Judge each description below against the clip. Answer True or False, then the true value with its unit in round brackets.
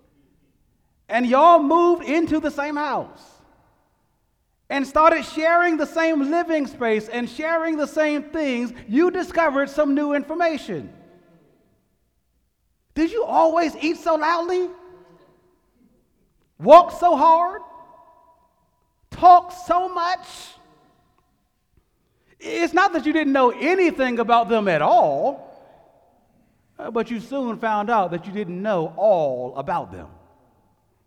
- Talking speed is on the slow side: True (115 wpm)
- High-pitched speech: True (300 Hz)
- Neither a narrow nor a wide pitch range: False (6.7 semitones)